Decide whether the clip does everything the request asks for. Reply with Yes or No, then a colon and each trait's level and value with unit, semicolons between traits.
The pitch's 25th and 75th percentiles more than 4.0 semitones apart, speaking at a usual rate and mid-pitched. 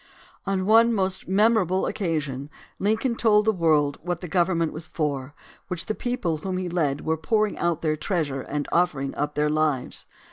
Yes: average, 4.5 semitones; average, 180 wpm; medium, 170 Hz